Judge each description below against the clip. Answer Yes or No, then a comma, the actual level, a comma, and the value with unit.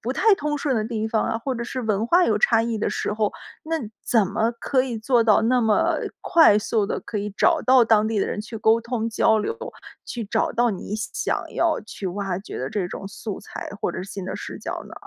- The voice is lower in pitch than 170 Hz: No, high, 225 Hz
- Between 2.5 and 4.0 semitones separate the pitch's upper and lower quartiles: Yes, average, 3.0 semitones